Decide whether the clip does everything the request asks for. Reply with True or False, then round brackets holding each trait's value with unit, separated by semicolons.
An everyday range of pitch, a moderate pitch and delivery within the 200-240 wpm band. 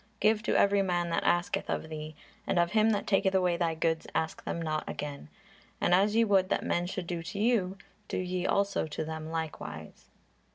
True (3.6 semitones; 175 Hz; 205 wpm)